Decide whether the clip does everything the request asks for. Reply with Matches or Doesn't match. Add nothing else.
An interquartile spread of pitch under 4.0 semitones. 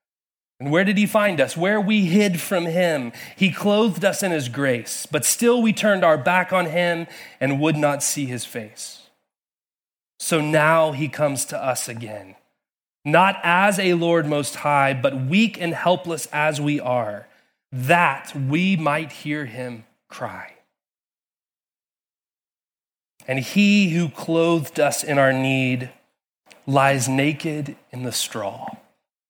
Doesn't match